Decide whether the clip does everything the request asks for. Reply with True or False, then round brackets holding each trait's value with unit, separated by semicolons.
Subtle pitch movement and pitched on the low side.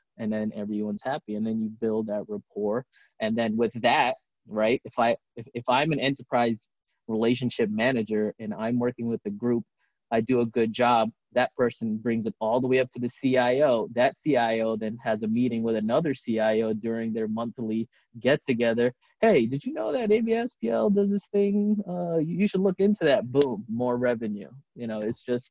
False (3.7 semitones; 120 Hz)